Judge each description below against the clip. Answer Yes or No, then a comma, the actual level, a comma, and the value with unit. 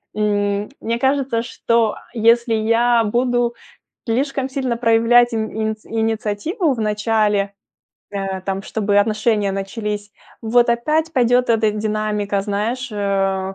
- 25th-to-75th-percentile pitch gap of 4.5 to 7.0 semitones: No, narrow, 2.6 semitones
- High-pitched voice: Yes, high, 220 Hz